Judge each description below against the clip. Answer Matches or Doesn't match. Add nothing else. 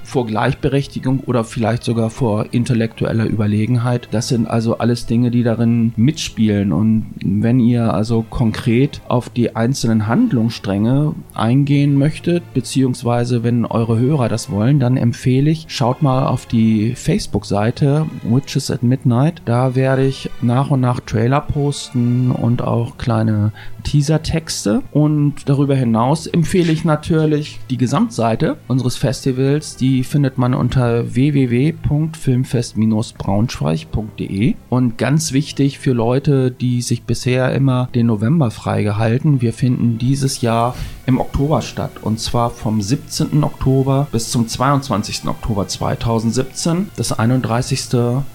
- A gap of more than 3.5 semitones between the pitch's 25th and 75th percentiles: Doesn't match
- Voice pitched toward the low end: Matches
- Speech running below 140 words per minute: Matches